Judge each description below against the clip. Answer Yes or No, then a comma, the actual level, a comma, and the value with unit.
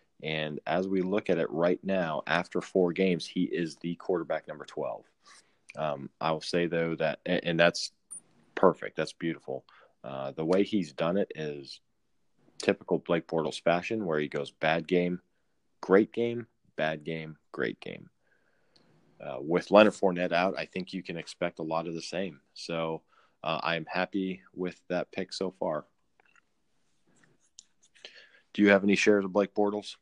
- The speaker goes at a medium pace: Yes, average, 165 wpm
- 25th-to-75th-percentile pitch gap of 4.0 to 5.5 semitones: No, average, 3.1 semitones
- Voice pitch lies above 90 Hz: No, very low, 85 Hz